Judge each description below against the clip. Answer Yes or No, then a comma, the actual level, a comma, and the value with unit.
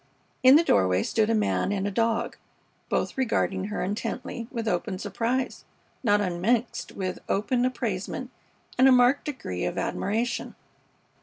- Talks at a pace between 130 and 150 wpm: Yes, average, 145 wpm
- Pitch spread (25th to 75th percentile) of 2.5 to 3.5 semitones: No, average, 4.2 semitones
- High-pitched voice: Yes, high, 225 Hz